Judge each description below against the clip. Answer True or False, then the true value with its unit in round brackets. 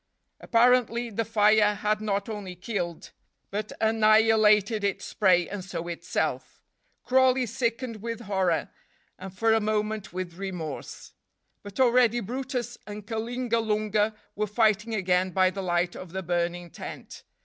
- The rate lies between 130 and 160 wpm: True (135 wpm)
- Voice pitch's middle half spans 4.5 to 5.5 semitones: False (3.2 semitones)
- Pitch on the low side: False (210 Hz)